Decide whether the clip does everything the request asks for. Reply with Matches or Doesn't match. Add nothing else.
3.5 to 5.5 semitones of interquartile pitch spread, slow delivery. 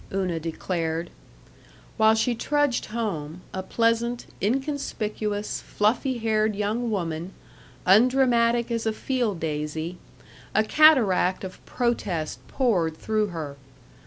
Matches